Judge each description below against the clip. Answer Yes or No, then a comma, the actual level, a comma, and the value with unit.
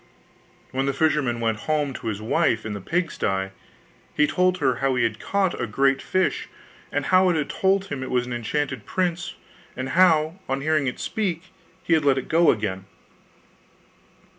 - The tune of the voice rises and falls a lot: Yes, wide, 5.8 semitones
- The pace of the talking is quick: No, average, 185 wpm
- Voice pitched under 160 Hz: Yes, medium, 140 Hz